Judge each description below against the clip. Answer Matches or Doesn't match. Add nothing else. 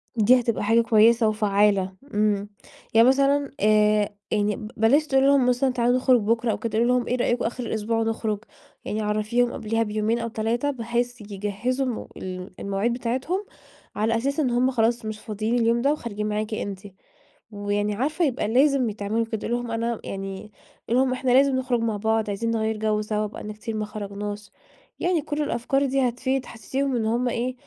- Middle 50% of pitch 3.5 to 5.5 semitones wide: Doesn't match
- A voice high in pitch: Matches